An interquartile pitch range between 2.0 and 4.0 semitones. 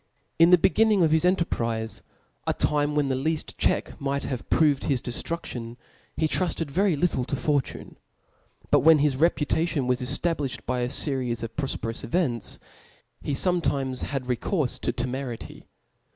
No: average, 4.4 semitones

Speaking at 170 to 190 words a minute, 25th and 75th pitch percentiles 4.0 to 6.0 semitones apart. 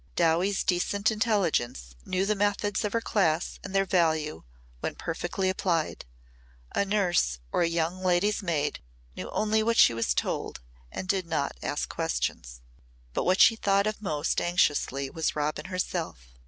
No: average, 155 wpm; average, 4.4 semitones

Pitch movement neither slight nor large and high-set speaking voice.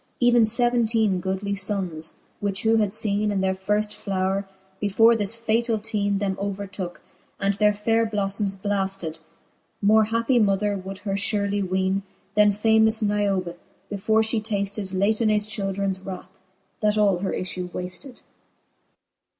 No: narrow, 2.1 semitones; high, 205 Hz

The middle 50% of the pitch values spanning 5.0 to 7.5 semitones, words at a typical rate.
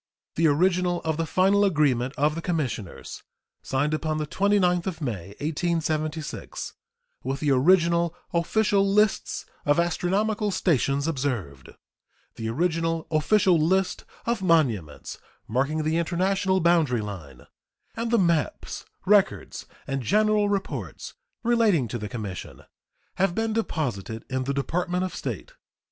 No: wide, 5.4 semitones; slow, 125 wpm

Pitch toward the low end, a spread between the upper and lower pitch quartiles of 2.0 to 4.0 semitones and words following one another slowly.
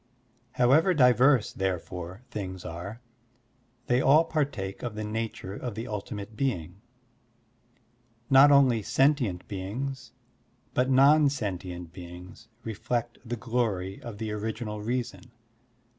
No: low, 110 Hz; average, 4.9 semitones; slow, 115 wpm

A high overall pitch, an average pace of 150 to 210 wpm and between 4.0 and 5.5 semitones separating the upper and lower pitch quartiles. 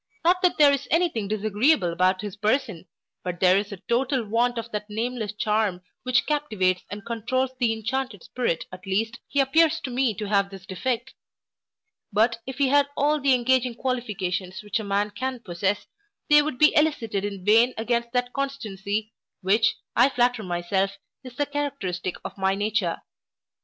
Yes: high, 225 Hz; average, 175 wpm; average, 4.7 semitones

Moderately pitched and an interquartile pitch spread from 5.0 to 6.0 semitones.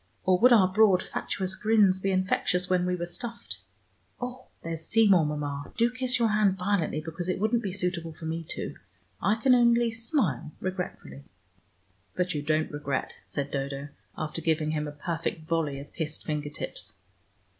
Yes: medium, 180 Hz; wide, 5.5 semitones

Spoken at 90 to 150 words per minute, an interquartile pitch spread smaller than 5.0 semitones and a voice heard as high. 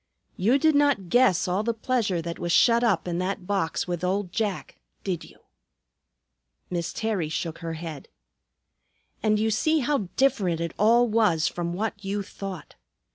No: average, 165 wpm; average, 4.6 semitones; high, 195 Hz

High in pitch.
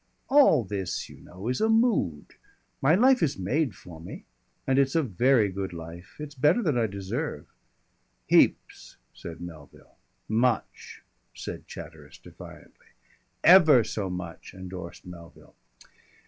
No: low, 110 Hz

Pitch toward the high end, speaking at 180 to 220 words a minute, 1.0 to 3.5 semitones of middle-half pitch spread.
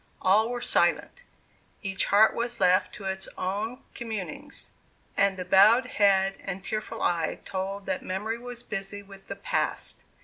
No: high, 200 Hz; average, 150 wpm; average, 2.8 semitones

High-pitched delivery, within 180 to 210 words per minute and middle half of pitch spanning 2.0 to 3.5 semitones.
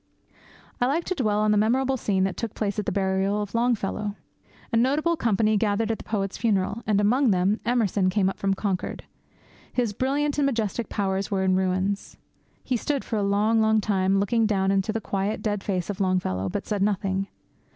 Yes: high, 205 Hz; average, 200 wpm; average, 2.8 semitones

